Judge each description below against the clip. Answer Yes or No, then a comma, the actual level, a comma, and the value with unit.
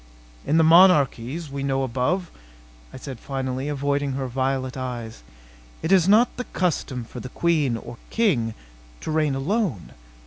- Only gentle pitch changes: No, average, 4.5 semitones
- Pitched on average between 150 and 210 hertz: No, medium, 140 Hz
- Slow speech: No, average, 150 wpm